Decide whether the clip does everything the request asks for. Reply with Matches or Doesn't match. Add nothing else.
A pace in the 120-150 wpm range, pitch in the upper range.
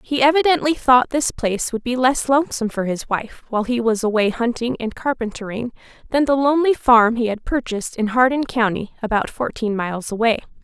Doesn't match